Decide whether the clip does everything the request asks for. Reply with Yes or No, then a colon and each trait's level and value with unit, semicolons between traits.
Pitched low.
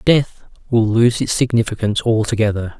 Yes: low, 115 Hz